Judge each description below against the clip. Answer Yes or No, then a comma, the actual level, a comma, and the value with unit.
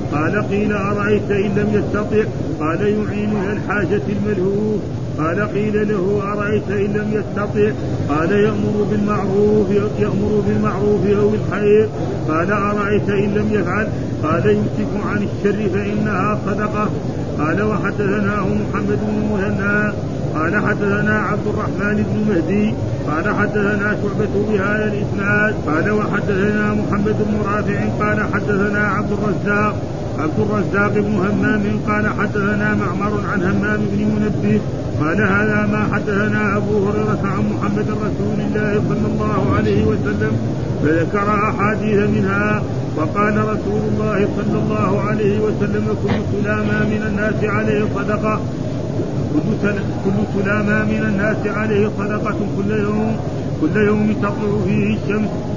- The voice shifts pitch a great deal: Yes, wide, 7.6 semitones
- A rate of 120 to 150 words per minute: Yes, average, 125 wpm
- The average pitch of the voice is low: No, high, 195 Hz